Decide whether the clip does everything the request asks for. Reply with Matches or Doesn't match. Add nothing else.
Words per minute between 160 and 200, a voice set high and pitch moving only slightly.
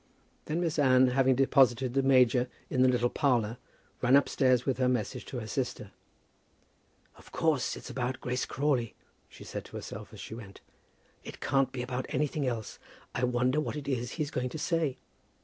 Doesn't match